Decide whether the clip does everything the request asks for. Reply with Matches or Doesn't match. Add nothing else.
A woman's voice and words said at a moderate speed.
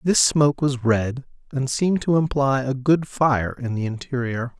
Doesn't match